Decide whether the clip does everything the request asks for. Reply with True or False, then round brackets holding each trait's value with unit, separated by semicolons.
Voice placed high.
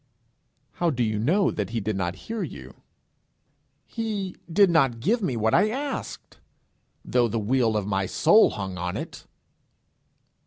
False (120 Hz)